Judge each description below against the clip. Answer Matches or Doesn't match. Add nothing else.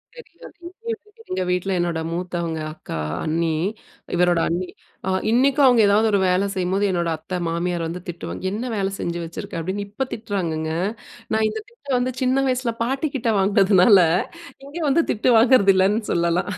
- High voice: Matches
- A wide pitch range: Matches